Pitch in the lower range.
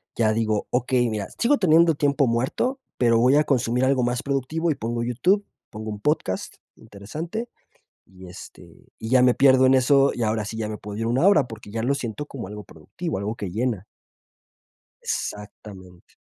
Yes: low, 120 Hz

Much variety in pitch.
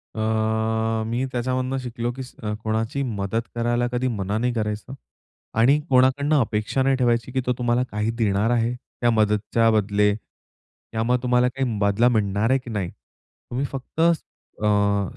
No: average, 2.8 semitones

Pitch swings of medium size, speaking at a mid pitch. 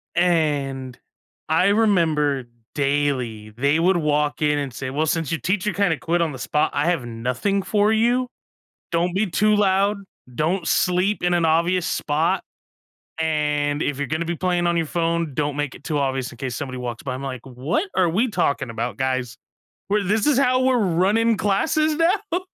No: wide, 5.7 semitones; medium, 165 Hz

